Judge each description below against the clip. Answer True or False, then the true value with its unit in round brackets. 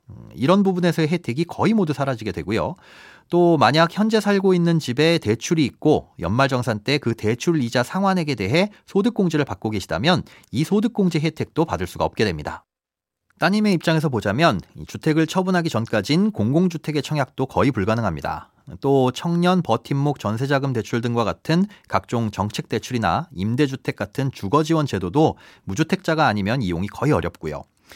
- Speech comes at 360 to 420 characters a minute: True (370 characters per minute)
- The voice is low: False (145 Hz)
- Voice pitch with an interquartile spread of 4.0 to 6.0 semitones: False (7.3 semitones)